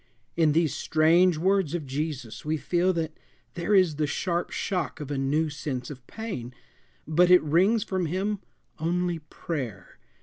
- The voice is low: No, medium, 160 Hz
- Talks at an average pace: Yes, average, 160 wpm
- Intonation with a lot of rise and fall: No, average, 3.4 semitones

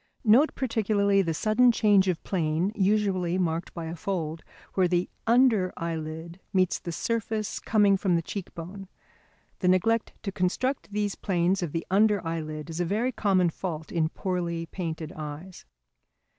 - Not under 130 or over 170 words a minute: Yes, average, 155 wpm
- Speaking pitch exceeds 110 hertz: Yes, medium, 185 Hz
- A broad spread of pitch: No, average, 3.7 semitones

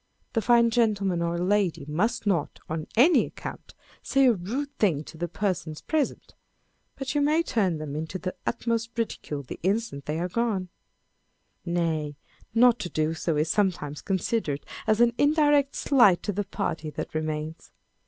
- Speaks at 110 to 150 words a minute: No, average, 165 wpm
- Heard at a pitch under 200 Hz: Yes, high, 190 Hz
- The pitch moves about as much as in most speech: No, wide, 6.7 semitones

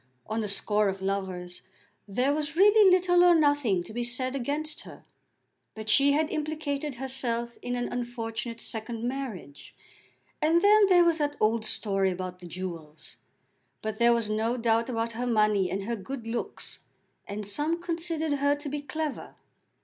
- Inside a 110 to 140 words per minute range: No, average, 165 wpm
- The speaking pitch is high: Yes, high, 240 Hz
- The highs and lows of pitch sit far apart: Yes, wide, 5.7 semitones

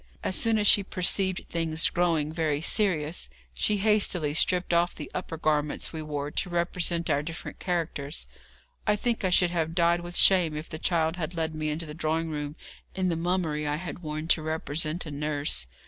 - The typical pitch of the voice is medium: Yes, medium, 165 Hz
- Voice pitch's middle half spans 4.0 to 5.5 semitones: No, narrow, 2.6 semitones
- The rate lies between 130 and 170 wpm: No, average, 195 wpm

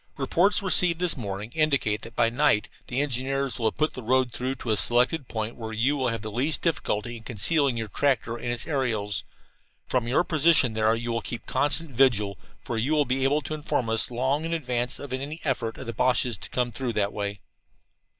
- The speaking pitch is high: No, low, 125 Hz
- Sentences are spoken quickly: Yes, fast, 215 wpm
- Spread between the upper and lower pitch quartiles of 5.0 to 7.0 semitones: No, average, 3.9 semitones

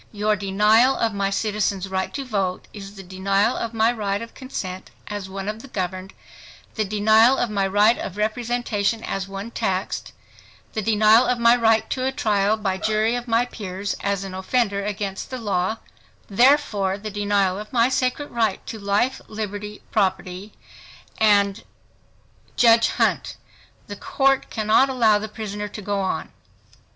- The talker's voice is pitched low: No, high, 210 Hz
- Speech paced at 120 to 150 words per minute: No, average, 160 wpm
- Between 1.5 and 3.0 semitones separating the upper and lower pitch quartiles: Yes, average, 2.7 semitones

